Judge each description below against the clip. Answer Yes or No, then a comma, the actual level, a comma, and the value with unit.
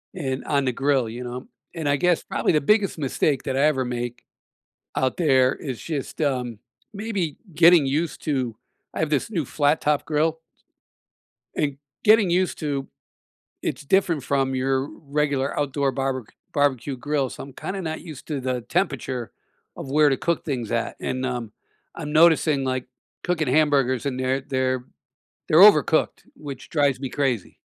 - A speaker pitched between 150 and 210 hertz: No, medium, 140 Hz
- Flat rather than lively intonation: No, average, 3.1 semitones